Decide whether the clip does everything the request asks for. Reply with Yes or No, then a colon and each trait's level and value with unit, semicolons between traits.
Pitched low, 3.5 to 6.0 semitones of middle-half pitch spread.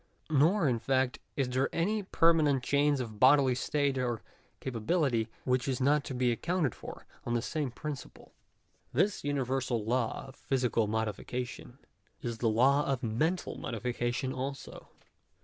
No: low, 130 Hz; average, 3.0 semitones